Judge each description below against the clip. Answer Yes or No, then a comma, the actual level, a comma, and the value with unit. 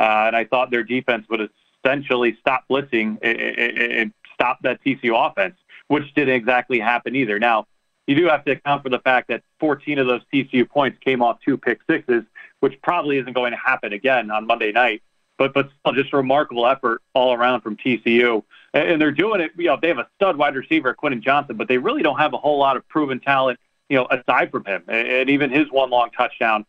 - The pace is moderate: No, fast, 225 wpm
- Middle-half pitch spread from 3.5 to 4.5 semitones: No, average, 2.9 semitones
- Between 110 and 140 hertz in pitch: Yes, low, 130 Hz